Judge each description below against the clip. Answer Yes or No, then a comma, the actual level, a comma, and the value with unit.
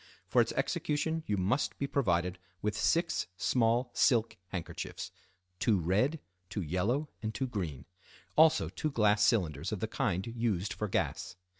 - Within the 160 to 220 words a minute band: No, average, 150 wpm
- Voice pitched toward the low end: Yes, low, 110 Hz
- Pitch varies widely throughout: Yes, wide, 6.0 semitones